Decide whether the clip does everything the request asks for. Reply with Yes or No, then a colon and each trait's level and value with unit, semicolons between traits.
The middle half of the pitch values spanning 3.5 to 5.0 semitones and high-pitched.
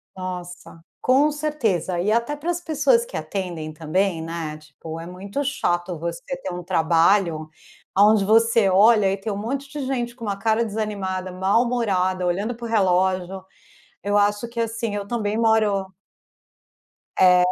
Yes: average, 4.2 semitones; high, 200 Hz